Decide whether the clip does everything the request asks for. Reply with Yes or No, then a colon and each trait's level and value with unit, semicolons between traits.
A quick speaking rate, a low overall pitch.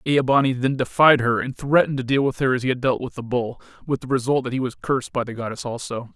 Yes: fast, 285 wpm; low, 130 Hz